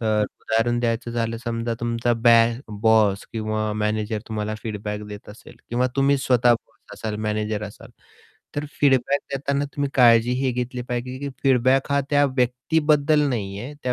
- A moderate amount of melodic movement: Yes, average, 3.1 semitones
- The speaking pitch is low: Yes, low, 120 Hz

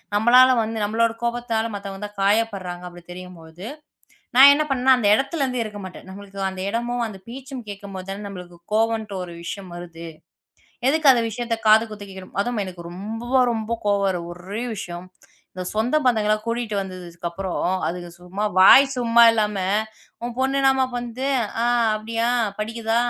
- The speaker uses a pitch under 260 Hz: Yes, high, 215 Hz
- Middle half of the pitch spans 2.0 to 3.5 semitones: No, average, 3.9 semitones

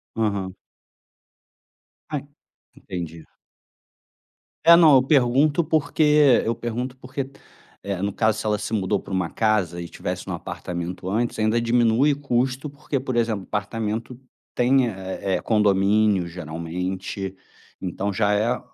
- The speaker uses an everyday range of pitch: Yes, average, 5.0 semitones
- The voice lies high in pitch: No, low, 110 Hz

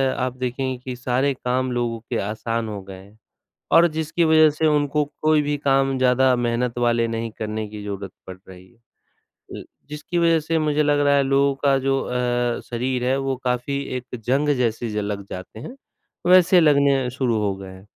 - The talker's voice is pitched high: No, low, 125 Hz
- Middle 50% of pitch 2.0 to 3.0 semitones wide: No, average, 3.6 semitones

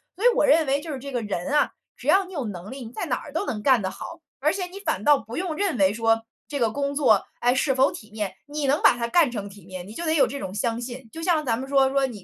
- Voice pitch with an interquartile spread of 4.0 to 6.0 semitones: Yes, average, 5.2 semitones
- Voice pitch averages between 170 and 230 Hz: No, very high, 265 Hz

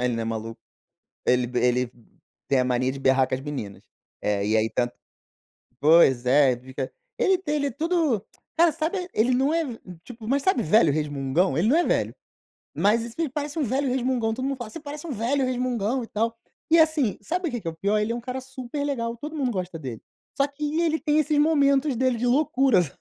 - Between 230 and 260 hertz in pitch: Yes, high, 240 Hz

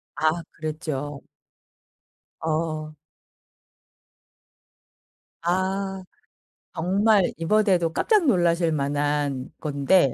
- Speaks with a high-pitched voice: No, medium, 165 Hz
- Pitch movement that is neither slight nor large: Yes, average, 4.3 semitones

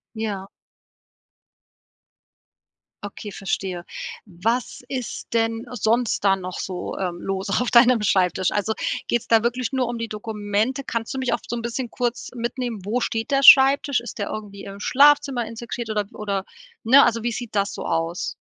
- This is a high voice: Yes, high, 225 Hz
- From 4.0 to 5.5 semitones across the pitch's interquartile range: No, average, 3.3 semitones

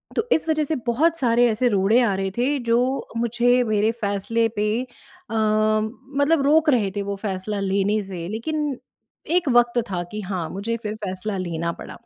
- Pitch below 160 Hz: No, high, 220 Hz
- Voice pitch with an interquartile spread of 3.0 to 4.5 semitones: Yes, average, 3.9 semitones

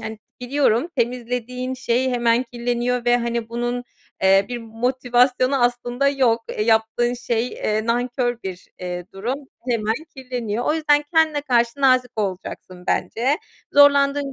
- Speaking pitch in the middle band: No, high, 245 Hz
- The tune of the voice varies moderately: No, narrow, 2.0 semitones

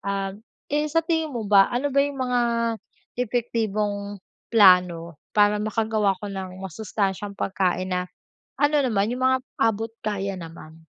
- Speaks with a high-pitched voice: Yes, high, 210 Hz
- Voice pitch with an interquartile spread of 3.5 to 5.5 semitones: Yes, average, 4.1 semitones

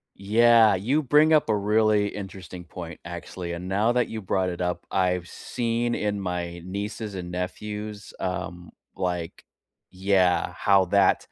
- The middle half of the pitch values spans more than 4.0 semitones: No, average, 3.1 semitones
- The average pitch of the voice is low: Yes, very low, 95 Hz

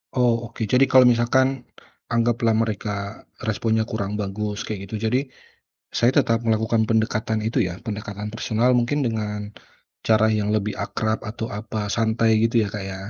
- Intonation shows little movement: Yes, narrow, 1.7 semitones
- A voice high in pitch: No, low, 110 Hz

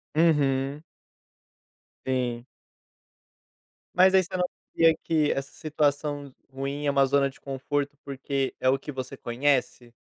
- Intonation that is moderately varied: No, narrow, 1.8 semitones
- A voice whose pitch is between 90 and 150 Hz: Yes, medium, 140 Hz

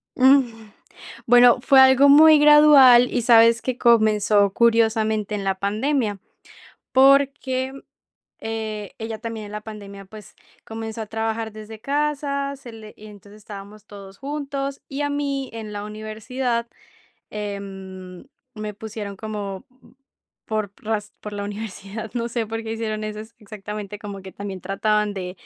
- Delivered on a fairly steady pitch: No, average, 3.2 semitones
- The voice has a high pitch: Yes, high, 220 Hz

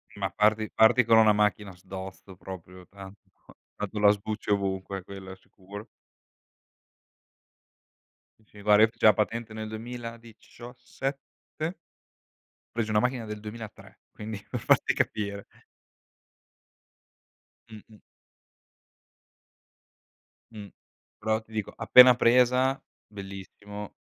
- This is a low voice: Yes, low, 105 Hz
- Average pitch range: No, narrow, 2.3 semitones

